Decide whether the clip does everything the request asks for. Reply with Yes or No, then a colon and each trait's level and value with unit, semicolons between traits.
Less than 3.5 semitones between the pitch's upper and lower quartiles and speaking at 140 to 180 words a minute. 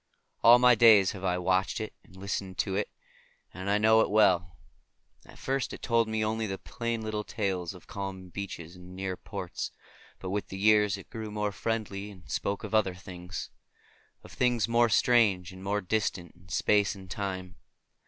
No: average, 2.8 semitones; average, 195 wpm